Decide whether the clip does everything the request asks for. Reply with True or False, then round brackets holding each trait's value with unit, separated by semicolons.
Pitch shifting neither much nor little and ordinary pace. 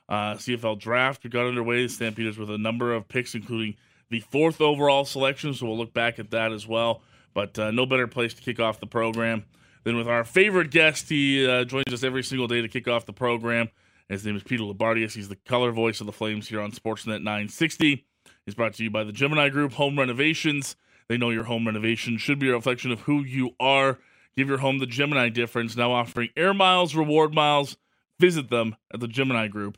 False (3.3 semitones; 220 wpm)